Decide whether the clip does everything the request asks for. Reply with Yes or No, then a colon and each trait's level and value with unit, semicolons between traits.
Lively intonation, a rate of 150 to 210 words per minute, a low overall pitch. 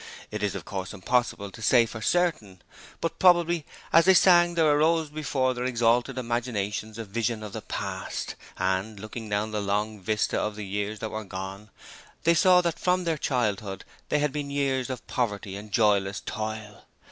Yes: wide, 6.0 semitones; average, 180 wpm; low, 115 Hz